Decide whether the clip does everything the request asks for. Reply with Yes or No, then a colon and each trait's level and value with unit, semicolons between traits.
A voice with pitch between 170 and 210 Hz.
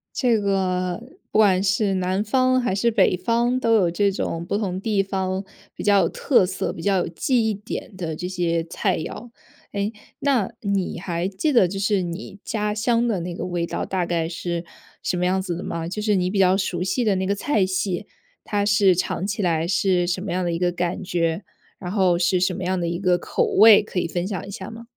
Yes: high, 190 Hz